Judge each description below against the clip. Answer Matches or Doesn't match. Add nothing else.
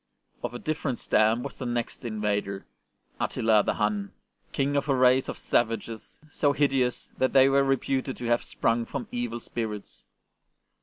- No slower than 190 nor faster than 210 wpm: Doesn't match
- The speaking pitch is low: Matches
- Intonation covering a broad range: Doesn't match